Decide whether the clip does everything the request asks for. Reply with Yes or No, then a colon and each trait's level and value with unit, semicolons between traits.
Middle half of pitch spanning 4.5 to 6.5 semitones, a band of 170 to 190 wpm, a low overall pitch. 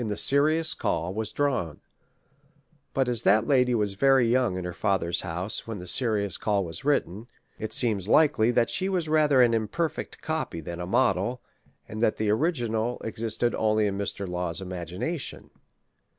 Yes: average, 5.0 semitones; average, 175 wpm; low, 110 Hz